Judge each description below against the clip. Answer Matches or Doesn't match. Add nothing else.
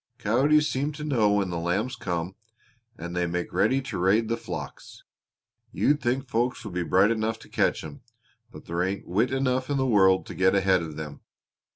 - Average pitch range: Doesn't match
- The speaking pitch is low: Matches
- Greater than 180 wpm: Matches